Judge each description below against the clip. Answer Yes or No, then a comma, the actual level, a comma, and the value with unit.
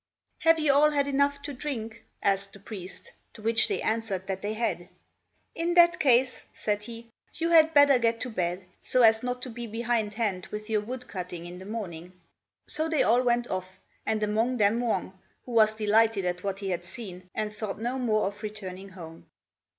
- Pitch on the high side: Yes, high, 220 Hz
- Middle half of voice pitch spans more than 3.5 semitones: Yes, average, 4.2 semitones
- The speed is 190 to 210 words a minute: Yes, average, 195 wpm